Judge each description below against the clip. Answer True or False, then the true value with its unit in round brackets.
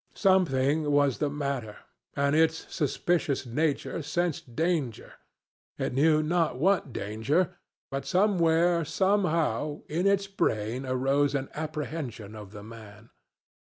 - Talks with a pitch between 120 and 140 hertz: False (150 Hz)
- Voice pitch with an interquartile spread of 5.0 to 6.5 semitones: False (4.6 semitones)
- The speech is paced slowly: True (115 wpm)